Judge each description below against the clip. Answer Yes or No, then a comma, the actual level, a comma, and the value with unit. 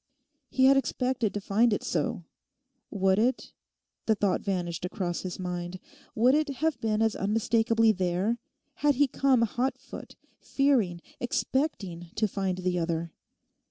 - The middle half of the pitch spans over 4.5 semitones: Yes, wide, 5.5 semitones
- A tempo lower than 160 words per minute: Yes, average, 145 wpm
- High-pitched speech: Yes, high, 215 Hz